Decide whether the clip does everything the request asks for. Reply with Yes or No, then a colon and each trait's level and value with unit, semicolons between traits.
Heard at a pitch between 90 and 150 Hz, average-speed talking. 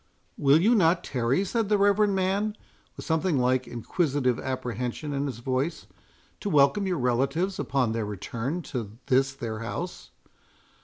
Yes: medium, 140 Hz; average, 150 wpm